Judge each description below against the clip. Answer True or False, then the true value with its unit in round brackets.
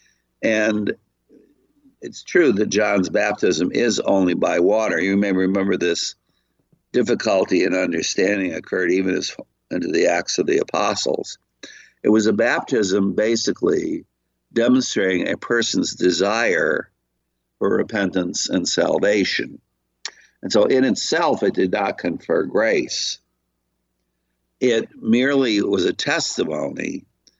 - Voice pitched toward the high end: False (95 Hz)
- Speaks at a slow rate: True (115 wpm)